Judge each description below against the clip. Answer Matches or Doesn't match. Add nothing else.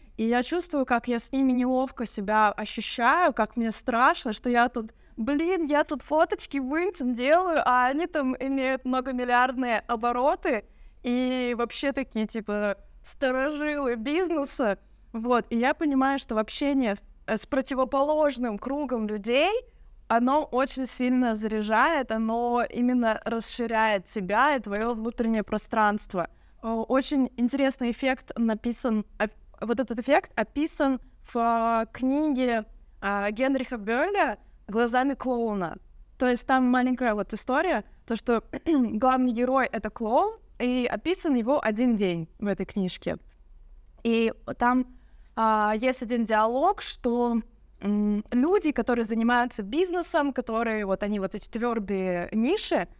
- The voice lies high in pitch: Matches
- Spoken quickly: Doesn't match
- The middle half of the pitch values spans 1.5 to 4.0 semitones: Matches